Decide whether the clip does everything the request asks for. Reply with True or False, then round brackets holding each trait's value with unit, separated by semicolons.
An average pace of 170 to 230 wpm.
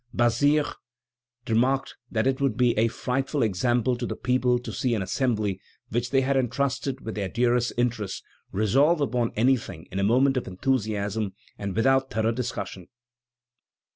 False (155 wpm)